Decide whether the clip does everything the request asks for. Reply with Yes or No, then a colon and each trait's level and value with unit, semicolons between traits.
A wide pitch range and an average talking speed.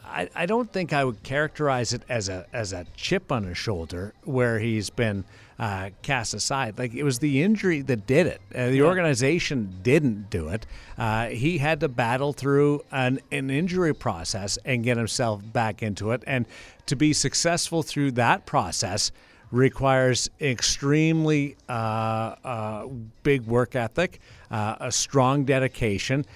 No: average, 4.4 semitones; average, 155 wpm